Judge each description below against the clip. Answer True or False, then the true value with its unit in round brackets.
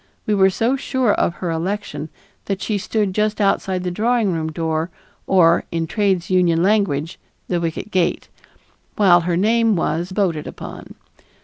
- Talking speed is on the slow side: False (165 wpm)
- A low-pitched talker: False (185 Hz)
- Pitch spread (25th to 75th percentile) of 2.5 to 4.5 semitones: True (3.7 semitones)